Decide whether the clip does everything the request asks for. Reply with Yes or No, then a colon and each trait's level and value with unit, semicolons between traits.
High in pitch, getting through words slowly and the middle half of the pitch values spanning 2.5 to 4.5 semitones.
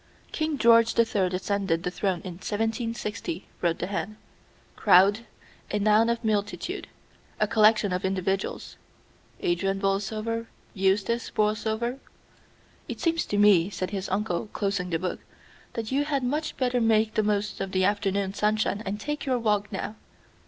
No: high, 210 Hz; average, 150 wpm; average, 2.8 semitones